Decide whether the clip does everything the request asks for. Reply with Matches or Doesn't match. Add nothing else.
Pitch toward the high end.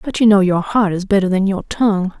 Matches